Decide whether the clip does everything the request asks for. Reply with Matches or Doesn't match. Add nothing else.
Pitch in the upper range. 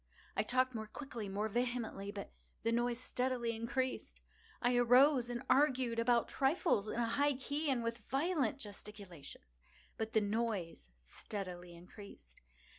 Matches